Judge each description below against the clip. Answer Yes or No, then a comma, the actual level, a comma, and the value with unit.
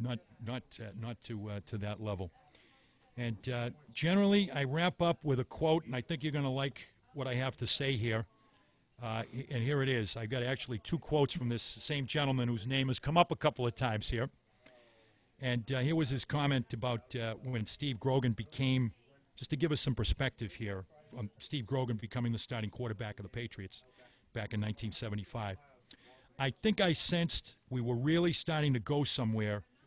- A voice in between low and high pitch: No, low, 125 Hz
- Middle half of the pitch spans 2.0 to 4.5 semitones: Yes, average, 3.4 semitones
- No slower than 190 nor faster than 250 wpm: Yes, average, 200 wpm